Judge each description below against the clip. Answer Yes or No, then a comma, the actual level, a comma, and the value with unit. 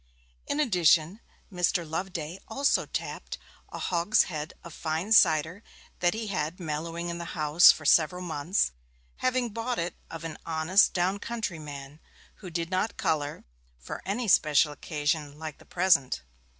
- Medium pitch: Yes, medium, 170 Hz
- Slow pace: No, average, 150 wpm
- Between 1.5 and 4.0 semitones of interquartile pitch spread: Yes, average, 3.5 semitones